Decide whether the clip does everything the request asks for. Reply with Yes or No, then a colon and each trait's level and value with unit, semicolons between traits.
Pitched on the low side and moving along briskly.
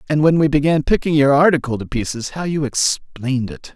No: medium, 145 Hz; fast, 210 wpm